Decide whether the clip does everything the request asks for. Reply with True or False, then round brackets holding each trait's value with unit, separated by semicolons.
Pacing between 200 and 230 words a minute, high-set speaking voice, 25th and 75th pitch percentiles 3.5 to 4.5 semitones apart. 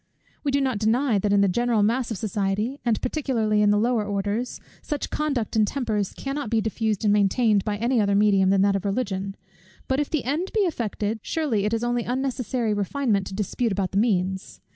True (205 wpm; 220 Hz; 3.8 semitones)